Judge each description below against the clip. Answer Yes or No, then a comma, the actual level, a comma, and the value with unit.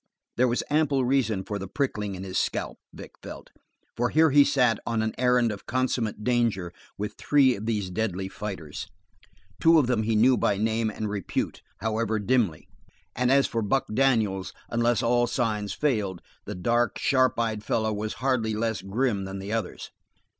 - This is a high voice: No, low, 115 Hz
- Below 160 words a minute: No, average, 175 wpm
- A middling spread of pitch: Yes, average, 3.3 semitones